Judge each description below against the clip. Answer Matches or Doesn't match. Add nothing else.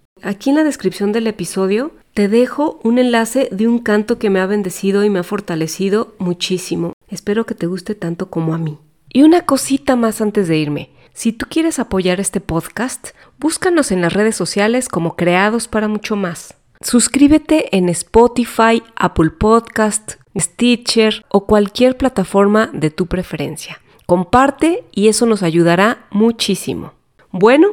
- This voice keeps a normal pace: Matches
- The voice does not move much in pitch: Doesn't match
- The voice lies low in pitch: Doesn't match